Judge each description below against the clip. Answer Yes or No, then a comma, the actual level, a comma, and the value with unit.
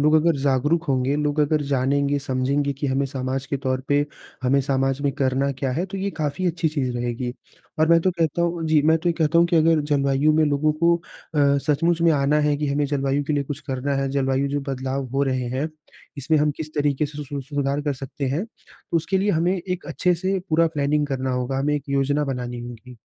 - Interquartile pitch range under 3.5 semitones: Yes, average, 2.7 semitones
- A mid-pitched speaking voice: Yes, medium, 145 Hz